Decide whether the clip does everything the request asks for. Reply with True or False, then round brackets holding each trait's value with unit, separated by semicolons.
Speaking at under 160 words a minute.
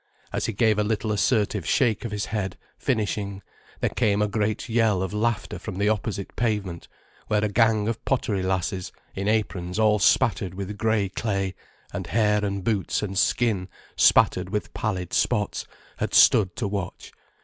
False (170 wpm)